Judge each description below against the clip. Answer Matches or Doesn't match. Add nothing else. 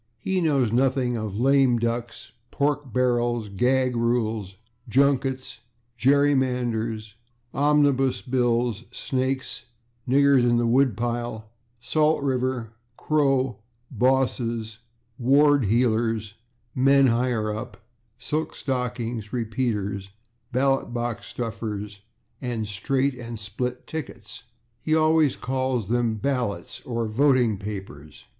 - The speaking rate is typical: Doesn't match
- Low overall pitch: Matches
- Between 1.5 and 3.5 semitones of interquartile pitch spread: Matches